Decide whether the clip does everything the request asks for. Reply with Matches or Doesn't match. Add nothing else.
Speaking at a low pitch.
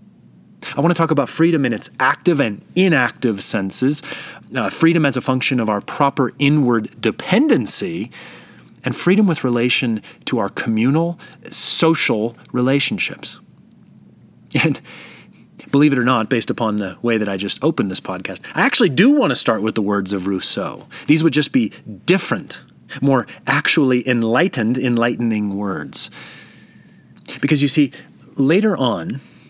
Matches